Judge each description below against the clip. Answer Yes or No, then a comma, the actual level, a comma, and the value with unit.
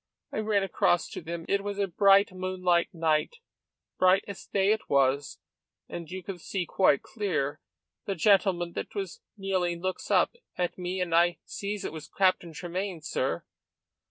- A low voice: No, medium, 185 Hz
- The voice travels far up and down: No, narrow, 2.6 semitones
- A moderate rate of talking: Yes, average, 165 wpm